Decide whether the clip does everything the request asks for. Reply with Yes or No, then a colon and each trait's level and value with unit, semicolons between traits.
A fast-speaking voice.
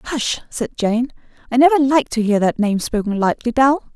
No: average, 195 wpm